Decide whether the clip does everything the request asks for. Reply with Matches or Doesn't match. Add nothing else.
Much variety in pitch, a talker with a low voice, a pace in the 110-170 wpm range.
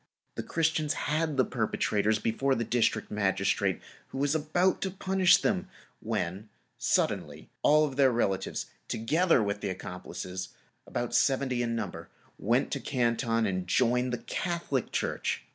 Matches